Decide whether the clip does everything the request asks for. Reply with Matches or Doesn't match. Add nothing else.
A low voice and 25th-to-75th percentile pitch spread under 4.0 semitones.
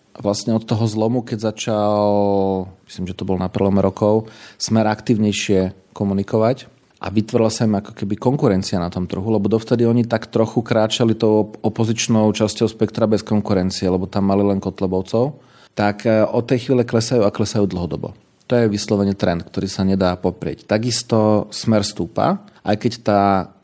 Matches